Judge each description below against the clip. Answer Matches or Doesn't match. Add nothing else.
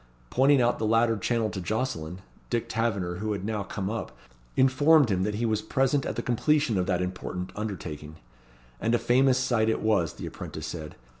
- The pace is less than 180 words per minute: Doesn't match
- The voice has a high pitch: Doesn't match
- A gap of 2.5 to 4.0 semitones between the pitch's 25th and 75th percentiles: Doesn't match